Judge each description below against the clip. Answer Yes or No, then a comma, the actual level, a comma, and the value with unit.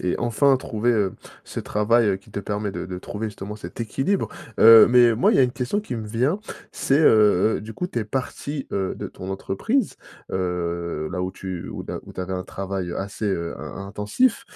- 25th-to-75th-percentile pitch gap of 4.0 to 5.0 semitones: Yes, average, 4.3 semitones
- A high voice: No, low, 105 Hz